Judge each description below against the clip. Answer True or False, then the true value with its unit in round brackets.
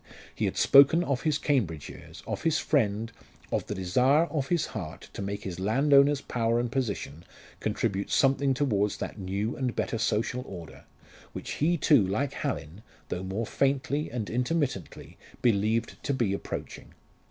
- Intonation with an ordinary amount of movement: False (5.7 semitones)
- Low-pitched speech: True (120 Hz)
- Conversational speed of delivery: True (160 wpm)